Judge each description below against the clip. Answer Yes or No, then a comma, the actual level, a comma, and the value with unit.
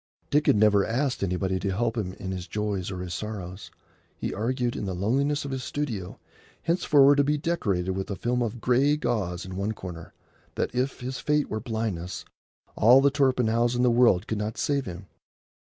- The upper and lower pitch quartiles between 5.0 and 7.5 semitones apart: Yes, wide, 5.4 semitones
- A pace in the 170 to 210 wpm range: Yes, average, 195 wpm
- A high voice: No, low, 110 Hz